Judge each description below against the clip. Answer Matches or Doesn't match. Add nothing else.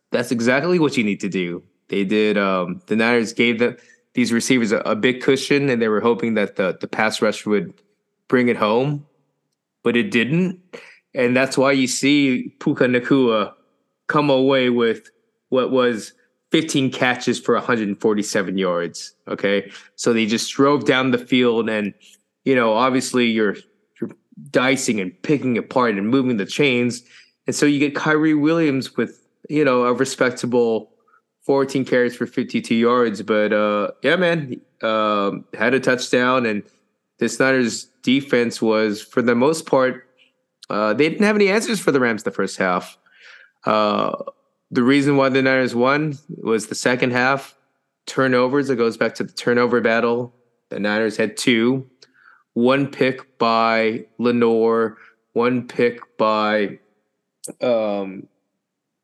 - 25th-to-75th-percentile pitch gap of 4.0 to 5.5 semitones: Doesn't match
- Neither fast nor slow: Matches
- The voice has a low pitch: Matches